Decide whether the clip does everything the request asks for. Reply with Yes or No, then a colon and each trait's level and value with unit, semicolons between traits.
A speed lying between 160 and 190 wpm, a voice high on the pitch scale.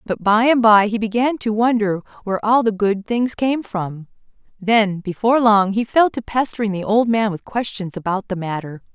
No: average, 200 wpm; high, 215 Hz